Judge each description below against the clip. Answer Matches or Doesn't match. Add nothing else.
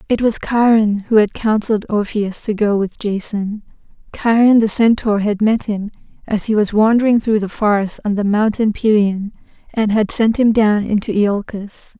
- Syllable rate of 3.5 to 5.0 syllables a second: Matches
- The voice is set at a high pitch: Matches